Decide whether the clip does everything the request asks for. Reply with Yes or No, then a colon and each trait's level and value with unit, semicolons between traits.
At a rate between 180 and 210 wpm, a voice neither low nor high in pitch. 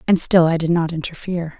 No: fast, 225 wpm; medium, 170 Hz